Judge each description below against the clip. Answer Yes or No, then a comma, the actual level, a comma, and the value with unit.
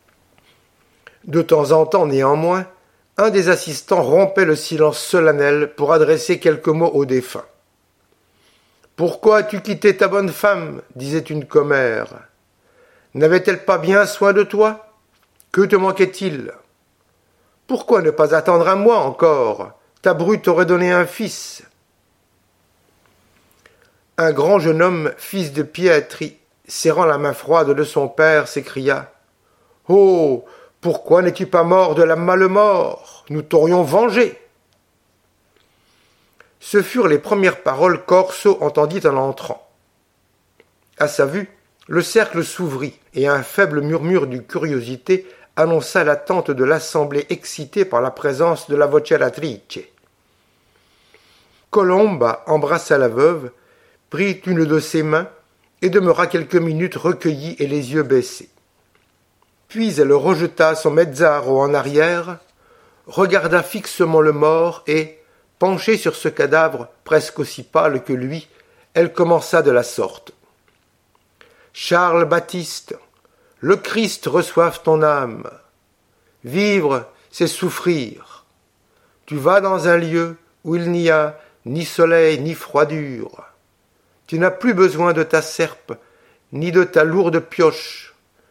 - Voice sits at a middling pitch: Yes, medium, 170 Hz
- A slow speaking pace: Yes, slow, 125 wpm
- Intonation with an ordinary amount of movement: Yes, average, 4.3 semitones